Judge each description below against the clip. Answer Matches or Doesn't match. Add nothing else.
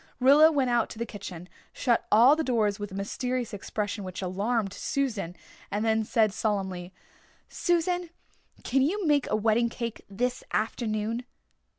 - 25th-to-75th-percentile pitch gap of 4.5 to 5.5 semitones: Doesn't match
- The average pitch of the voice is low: Doesn't match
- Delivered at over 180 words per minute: Doesn't match